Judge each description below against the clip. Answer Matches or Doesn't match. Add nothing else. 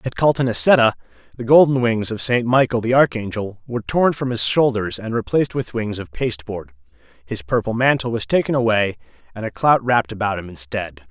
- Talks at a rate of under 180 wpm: Doesn't match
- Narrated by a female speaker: Doesn't match